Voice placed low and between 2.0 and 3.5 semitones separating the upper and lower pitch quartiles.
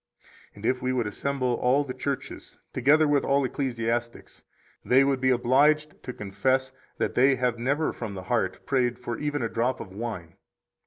Yes: low, 125 Hz; average, 2.7 semitones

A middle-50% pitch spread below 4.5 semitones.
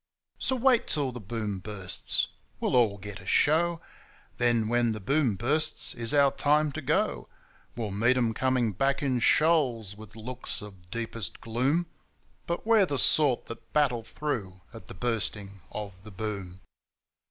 No: average, 5.3 semitones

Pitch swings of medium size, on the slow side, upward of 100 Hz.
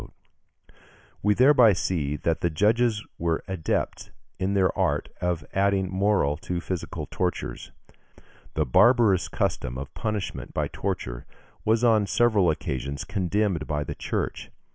No: average, 4.8 semitones; slow, 130 wpm; very low, 95 Hz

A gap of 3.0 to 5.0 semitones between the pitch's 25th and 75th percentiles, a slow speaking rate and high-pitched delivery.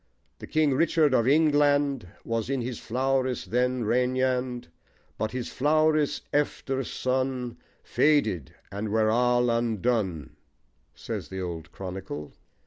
No: average, 3.6 semitones; slow, 120 wpm; low, 125 Hz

